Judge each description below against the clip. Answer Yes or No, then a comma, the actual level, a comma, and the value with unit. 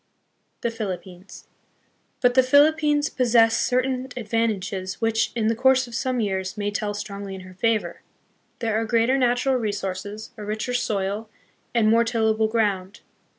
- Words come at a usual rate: Yes, average, 150 wpm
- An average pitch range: Yes, average, 3.3 semitones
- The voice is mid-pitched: No, high, 225 Hz